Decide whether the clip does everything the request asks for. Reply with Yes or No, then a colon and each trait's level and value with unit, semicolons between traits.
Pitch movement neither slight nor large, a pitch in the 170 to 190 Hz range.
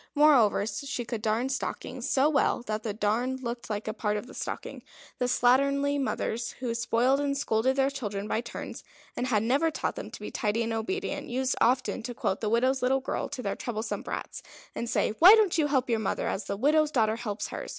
No: average, 3.6 semitones; high, 245 Hz